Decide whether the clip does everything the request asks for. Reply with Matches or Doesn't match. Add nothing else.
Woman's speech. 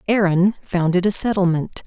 Matches